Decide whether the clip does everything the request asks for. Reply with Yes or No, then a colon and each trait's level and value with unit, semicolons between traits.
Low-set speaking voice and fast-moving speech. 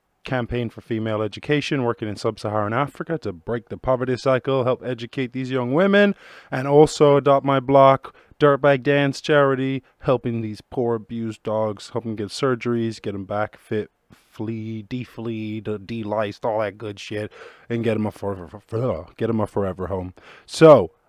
No: low, 115 Hz; average, 160 wpm